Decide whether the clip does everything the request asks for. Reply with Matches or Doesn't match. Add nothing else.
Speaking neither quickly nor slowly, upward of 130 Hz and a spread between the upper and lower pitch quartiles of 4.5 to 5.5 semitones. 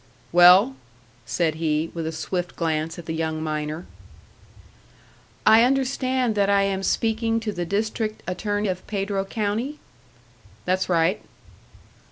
Doesn't match